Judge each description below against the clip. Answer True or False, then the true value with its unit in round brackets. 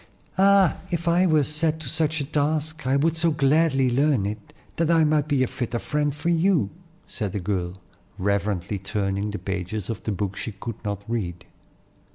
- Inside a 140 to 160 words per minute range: False (190 wpm)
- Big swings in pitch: True (7.5 semitones)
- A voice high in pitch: False (135 Hz)